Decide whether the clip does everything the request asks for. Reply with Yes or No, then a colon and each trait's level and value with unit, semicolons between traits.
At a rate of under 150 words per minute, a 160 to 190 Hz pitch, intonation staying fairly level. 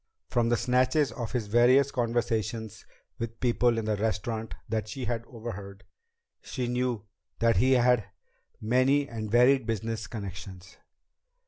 No: slow, 135 wpm; low, 115 Hz; narrow, 2.2 semitones